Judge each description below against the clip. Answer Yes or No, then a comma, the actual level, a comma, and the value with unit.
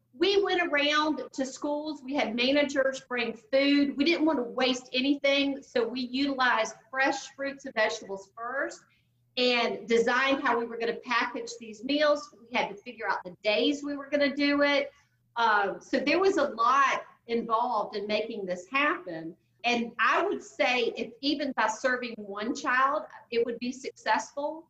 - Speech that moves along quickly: No, average, 175 wpm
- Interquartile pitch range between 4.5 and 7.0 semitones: No, average, 3.8 semitones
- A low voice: No, very high, 255 Hz